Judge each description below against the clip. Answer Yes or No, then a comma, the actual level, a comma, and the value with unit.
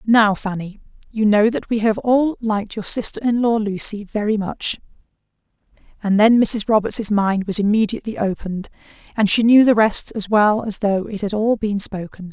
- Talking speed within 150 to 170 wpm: No, average, 185 wpm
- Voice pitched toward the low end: No, high, 210 Hz